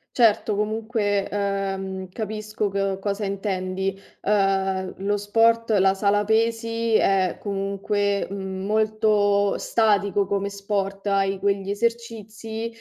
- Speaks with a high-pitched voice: Yes, high, 200 Hz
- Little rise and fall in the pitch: Yes, narrow, 1.8 semitones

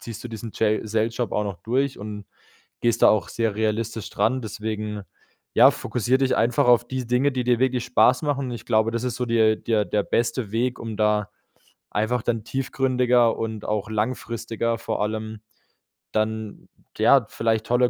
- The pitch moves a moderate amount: No, narrow, 2.2 semitones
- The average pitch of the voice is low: Yes, low, 115 Hz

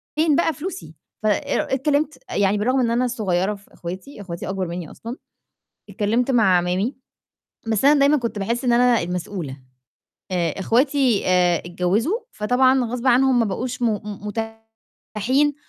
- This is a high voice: Yes, high, 230 Hz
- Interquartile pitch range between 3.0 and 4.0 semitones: No, wide, 5.5 semitones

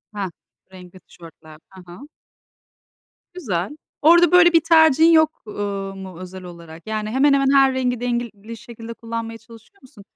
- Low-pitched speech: No, high, 230 Hz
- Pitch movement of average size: No, wide, 6.3 semitones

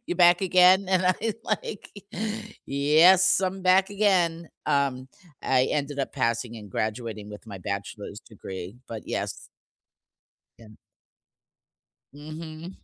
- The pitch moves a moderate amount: No, wide, 8.2 semitones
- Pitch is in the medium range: Yes, medium, 145 Hz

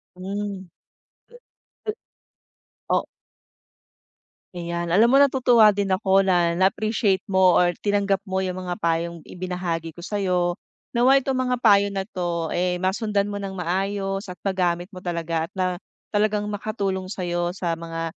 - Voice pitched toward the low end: No, high, 190 Hz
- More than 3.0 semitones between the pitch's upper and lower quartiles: No, narrow, 2.5 semitones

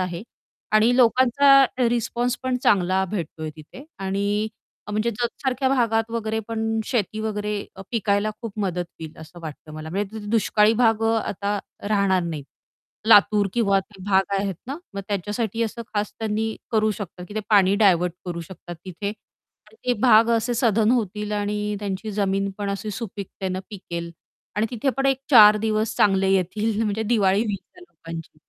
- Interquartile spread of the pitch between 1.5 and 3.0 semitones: Yes, average, 2.7 semitones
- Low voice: No, high, 210 Hz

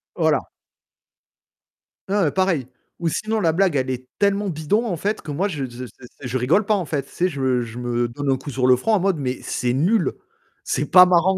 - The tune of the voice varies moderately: No, wide, 6.9 semitones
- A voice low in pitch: No, medium, 155 Hz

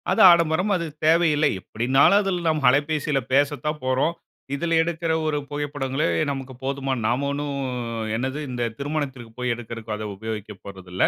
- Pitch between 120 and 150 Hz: Yes, medium, 140 Hz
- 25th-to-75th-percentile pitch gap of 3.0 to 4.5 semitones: Yes, average, 4.2 semitones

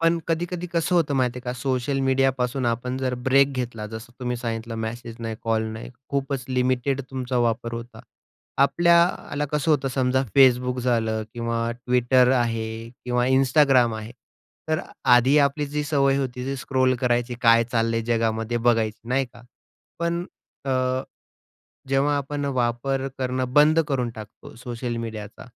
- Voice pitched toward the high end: No, low, 125 Hz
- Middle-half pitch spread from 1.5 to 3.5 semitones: Yes, average, 2.7 semitones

